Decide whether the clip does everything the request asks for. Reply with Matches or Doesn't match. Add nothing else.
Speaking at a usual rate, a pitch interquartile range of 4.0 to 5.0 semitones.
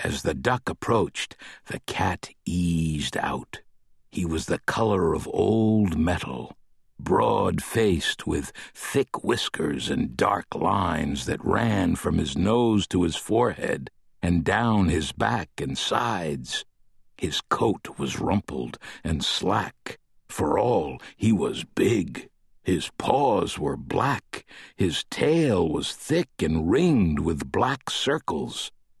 Doesn't match